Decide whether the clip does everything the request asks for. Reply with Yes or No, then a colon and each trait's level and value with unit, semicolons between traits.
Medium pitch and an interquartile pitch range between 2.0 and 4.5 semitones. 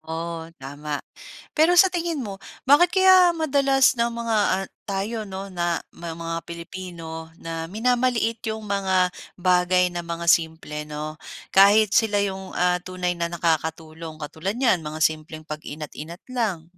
No: medium, 180 Hz; wide, 5.4 semitones